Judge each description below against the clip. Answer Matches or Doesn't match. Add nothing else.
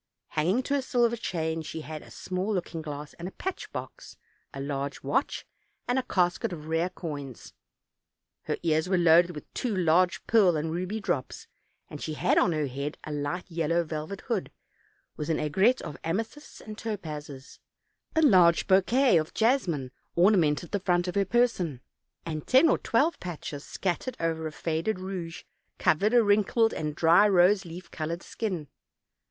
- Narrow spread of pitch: Doesn't match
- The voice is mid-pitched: Matches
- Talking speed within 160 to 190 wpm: Matches